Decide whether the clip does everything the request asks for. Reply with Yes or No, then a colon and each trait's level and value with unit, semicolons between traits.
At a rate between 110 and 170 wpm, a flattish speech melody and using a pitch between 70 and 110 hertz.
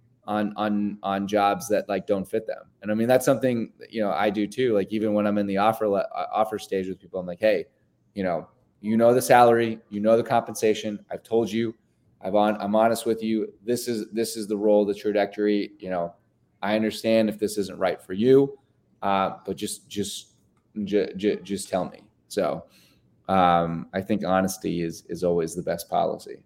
No: fast, 205 wpm; narrow, 2.2 semitones; low, 105 Hz